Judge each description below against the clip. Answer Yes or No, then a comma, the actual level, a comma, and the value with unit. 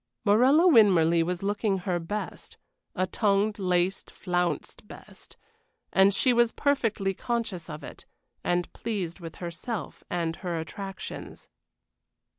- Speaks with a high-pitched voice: Yes, high, 195 Hz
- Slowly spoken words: Yes, slow, 120 wpm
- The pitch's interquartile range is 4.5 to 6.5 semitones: No, average, 3.5 semitones